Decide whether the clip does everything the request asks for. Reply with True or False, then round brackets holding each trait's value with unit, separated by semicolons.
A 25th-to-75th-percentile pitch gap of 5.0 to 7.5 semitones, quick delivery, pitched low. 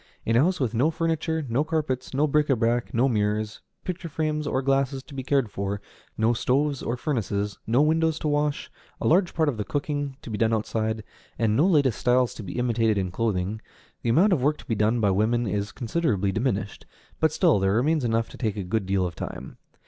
True (5.5 semitones; 220 wpm; 120 Hz)